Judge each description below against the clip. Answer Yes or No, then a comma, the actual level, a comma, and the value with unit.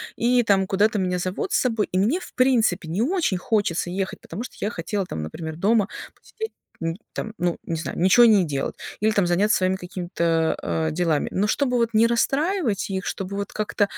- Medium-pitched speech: No, high, 195 Hz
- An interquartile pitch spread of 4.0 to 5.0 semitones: Yes, average, 4.3 semitones